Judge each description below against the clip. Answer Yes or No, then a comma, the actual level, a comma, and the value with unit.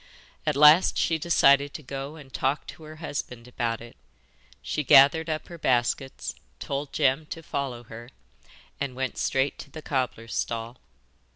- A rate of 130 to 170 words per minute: Yes, average, 160 wpm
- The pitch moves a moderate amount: Yes, average, 3.4 semitones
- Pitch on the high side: No, medium, 140 Hz